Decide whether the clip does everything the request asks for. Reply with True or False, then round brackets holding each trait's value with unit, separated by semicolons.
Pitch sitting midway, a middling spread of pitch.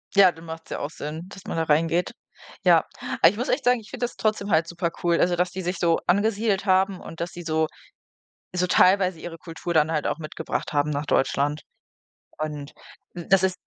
True (175 Hz; 3.1 semitones)